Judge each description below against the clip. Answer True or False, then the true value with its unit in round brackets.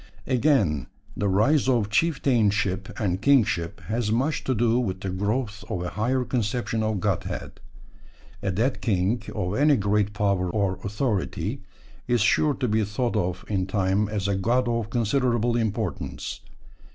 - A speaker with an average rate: True (150 wpm)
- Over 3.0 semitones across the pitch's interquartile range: True (3.8 semitones)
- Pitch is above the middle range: False (105 Hz)